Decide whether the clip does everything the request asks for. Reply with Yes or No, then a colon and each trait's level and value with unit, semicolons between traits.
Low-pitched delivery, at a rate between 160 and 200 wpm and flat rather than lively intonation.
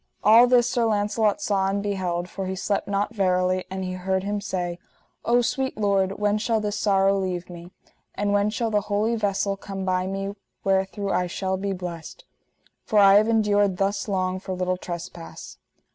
No: high, 195 Hz; average, 185 wpm; narrow, 1.9 semitones